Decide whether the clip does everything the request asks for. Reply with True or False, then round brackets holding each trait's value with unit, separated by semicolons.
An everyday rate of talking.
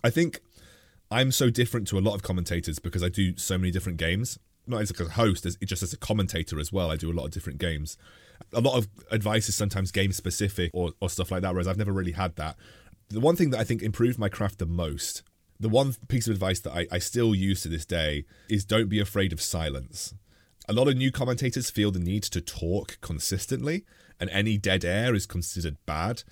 False (235 wpm)